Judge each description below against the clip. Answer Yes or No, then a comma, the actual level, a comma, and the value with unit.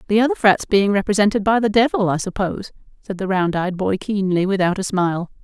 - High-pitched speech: Yes, high, 200 Hz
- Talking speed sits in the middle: No, fast, 210 wpm